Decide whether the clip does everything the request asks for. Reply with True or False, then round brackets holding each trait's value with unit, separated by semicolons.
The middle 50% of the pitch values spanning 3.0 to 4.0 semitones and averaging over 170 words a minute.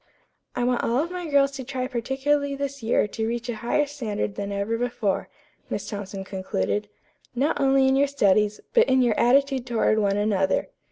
False (4.8 semitones; 180 wpm)